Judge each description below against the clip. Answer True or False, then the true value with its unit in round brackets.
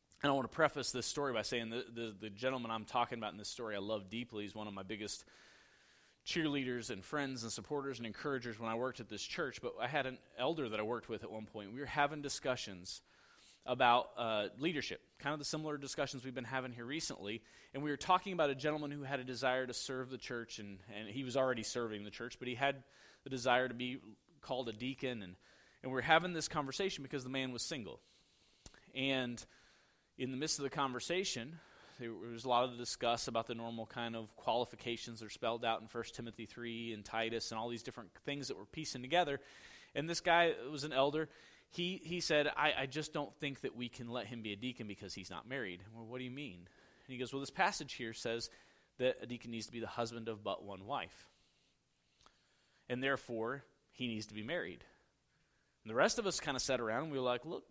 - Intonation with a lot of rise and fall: False (3.5 semitones)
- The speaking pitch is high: False (125 Hz)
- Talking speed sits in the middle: False (235 wpm)